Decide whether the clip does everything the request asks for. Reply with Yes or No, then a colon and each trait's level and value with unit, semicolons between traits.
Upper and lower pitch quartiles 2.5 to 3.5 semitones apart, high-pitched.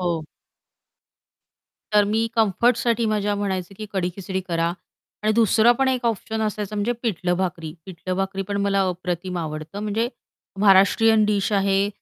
Yes: average, 2.9 semitones; high, 200 Hz